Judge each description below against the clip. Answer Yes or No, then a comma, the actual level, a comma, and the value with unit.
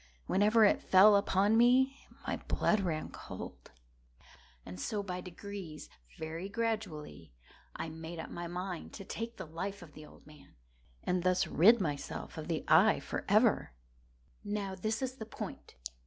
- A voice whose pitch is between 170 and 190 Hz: Yes, medium, 185 Hz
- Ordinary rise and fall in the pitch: Yes, average, 4.8 semitones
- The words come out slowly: No, average, 145 wpm